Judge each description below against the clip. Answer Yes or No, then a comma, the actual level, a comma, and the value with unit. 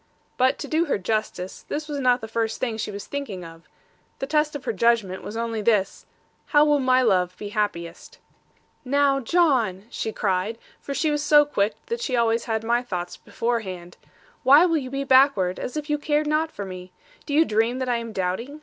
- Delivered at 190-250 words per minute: Yes, fast, 205 wpm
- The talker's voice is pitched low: No, high, 235 Hz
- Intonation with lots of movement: Yes, wide, 5.9 semitones